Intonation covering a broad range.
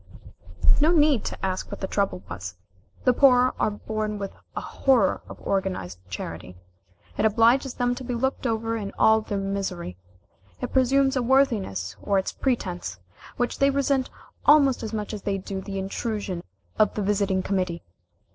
No: average, 4.8 semitones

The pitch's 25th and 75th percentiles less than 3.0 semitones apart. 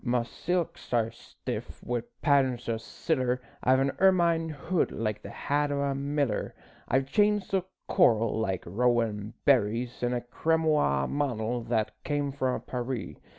No: average, 4.1 semitones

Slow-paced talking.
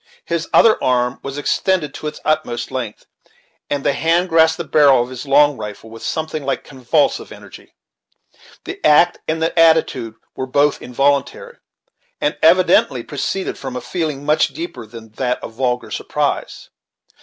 No: average, 155 wpm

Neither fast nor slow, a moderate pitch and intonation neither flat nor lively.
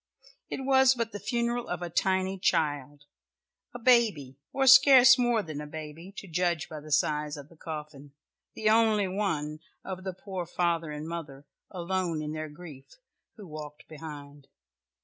No: average, 165 wpm; medium, 170 Hz; wide, 5.8 semitones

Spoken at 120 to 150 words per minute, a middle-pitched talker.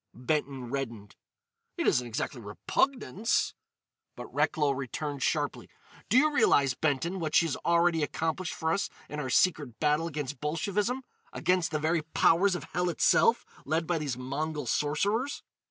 Yes: average, 140 wpm; medium, 155 Hz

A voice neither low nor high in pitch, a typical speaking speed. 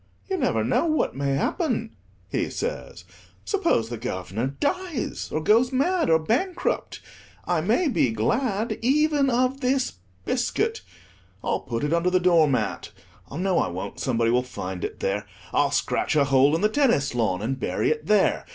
Yes: medium, 175 Hz; average, 165 wpm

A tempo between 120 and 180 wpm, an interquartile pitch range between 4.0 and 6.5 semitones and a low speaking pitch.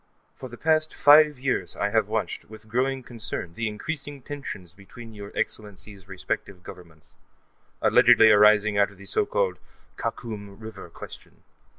Yes: average, 150 wpm; average, 4.3 semitones; low, 105 Hz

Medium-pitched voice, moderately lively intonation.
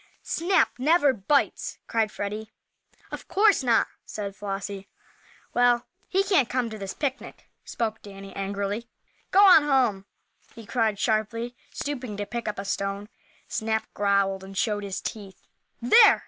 No: high, 220 Hz; average, 4.2 semitones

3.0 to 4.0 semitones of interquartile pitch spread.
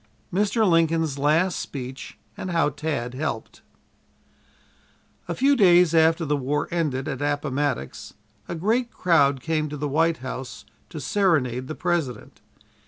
Yes: average, 3.7 semitones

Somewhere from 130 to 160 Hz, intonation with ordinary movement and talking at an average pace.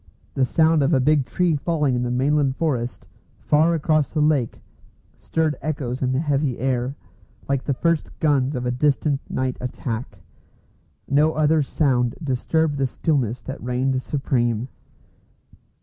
Yes: medium, 140 Hz; average, 3.2 semitones; average, 150 wpm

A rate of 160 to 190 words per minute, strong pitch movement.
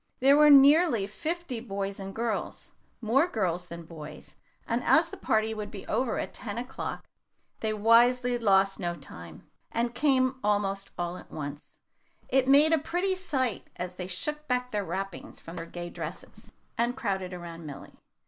Yes: average, 165 wpm; wide, 5.8 semitones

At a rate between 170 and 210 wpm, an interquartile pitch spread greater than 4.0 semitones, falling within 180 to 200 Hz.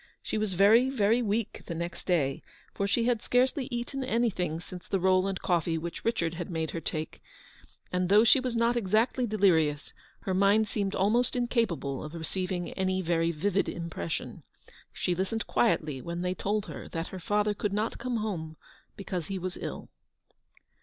Yes: average, 180 wpm; average, 4.5 semitones; high, 190 Hz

